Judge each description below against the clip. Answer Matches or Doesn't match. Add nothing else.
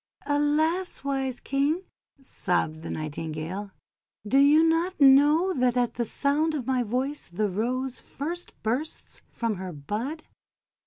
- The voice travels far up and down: Matches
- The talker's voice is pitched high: Matches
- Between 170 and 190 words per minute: Doesn't match